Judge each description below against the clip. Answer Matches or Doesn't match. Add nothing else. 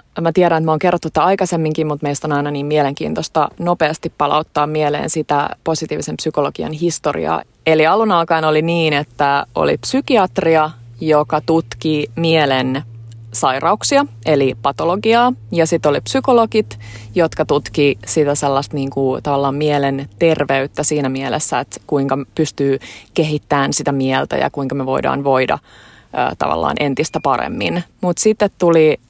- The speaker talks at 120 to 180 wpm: Matches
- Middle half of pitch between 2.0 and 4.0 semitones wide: Matches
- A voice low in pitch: Doesn't match